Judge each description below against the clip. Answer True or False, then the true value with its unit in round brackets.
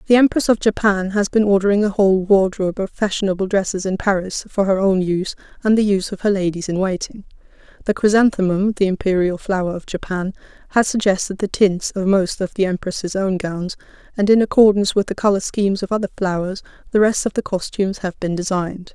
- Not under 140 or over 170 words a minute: False (200 wpm)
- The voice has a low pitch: False (195 Hz)